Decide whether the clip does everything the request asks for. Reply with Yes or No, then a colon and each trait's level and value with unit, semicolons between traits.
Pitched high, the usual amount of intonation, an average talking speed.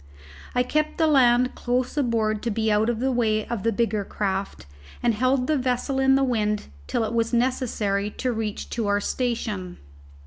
Yes: high, 235 Hz; average, 3.0 semitones; average, 185 wpm